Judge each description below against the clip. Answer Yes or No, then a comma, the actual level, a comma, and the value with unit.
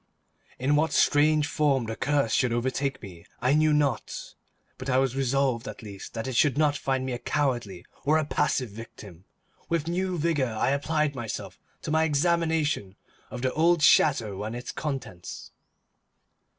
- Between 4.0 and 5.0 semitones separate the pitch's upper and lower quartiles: Yes, average, 4.3 semitones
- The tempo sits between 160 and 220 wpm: Yes, average, 165 wpm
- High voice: No, low, 135 Hz